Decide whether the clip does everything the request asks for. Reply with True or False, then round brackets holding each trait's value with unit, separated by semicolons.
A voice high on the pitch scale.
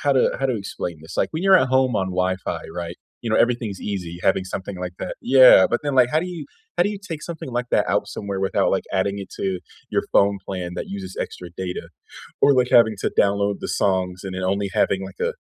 False (100 Hz)